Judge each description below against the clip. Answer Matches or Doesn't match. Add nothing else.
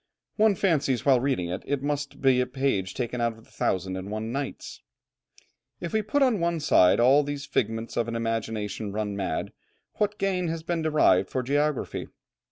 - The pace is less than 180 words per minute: Doesn't match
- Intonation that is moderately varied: Doesn't match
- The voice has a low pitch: Matches